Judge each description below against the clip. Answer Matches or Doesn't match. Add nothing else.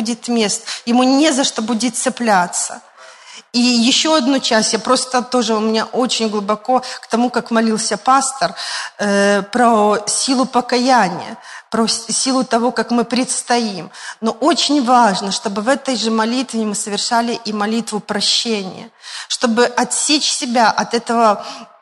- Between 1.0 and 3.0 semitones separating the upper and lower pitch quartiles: Matches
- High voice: Matches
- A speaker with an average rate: Matches